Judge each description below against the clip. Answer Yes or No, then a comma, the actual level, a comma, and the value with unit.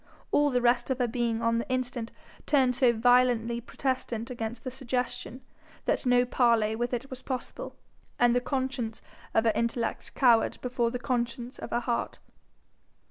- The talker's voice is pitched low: No, high, 245 Hz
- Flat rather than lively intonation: Yes, narrow, 1.4 semitones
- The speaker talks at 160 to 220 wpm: Yes, average, 165 wpm